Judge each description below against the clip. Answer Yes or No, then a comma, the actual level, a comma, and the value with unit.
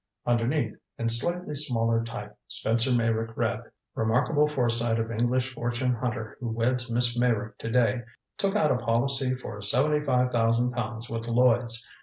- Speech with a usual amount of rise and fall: No, narrow, 1.8 semitones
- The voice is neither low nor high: No, low, 120 Hz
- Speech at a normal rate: Yes, average, 155 wpm